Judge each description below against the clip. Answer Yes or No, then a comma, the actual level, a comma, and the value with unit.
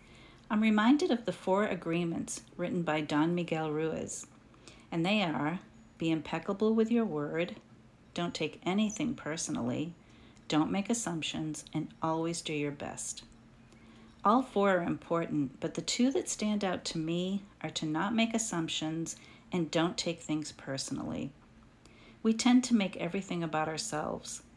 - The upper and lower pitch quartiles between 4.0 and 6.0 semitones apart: Yes, average, 4.7 semitones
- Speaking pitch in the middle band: Yes, medium, 165 Hz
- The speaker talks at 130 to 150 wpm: Yes, average, 145 wpm